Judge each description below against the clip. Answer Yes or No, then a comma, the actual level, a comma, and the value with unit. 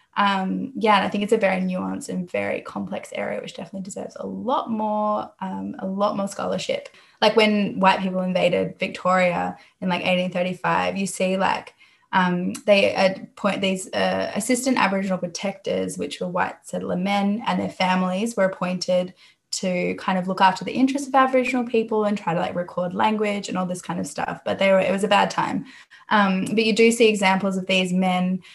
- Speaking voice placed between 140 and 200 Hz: Yes, high, 190 Hz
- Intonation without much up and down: Yes, narrow, 2.3 semitones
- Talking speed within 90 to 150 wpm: No, average, 195 wpm